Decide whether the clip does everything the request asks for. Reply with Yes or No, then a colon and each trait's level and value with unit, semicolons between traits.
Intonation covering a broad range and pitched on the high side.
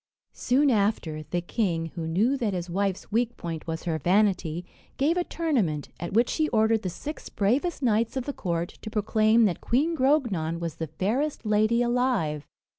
Yes: wide, 6.4 semitones; high, 215 Hz